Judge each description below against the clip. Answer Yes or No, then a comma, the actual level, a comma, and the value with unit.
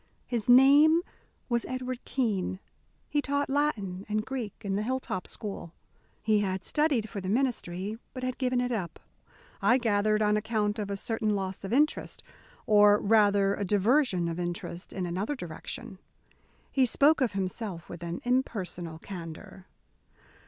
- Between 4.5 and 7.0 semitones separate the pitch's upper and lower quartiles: Yes, average, 5.0 semitones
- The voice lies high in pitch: Yes, high, 210 Hz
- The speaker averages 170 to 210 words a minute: No, average, 150 wpm